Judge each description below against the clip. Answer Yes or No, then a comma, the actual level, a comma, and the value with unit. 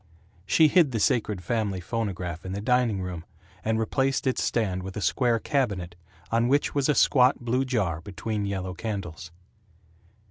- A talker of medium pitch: No, low, 110 Hz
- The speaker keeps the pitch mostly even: No, average, 5.1 semitones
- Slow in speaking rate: No, average, 165 wpm